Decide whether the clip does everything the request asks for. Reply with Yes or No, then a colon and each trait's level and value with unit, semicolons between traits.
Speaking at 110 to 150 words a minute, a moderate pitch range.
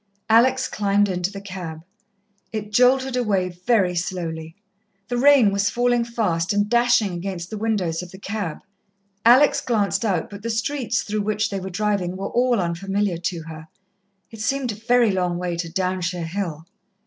No: average, 170 wpm; average, 4.3 semitones